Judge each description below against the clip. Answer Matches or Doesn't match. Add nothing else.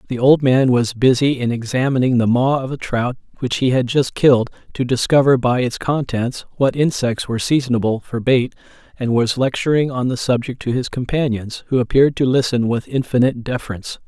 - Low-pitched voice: Matches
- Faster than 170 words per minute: Matches